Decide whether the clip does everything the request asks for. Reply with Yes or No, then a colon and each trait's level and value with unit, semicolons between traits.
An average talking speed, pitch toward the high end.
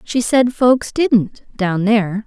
Yes: average, 160 wpm; high, 225 Hz